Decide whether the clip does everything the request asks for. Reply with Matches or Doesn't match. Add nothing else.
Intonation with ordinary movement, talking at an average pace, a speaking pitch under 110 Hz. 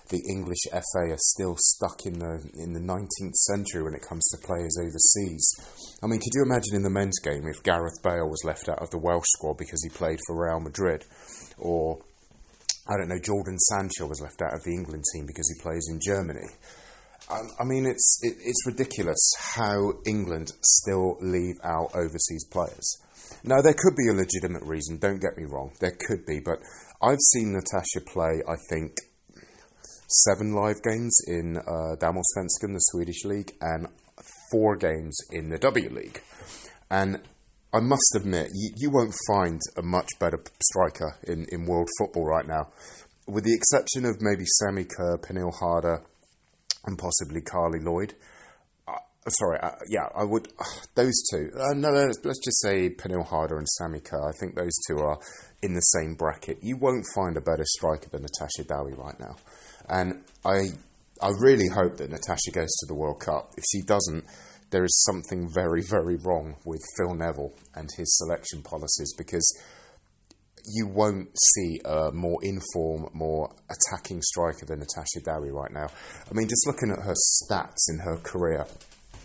Matches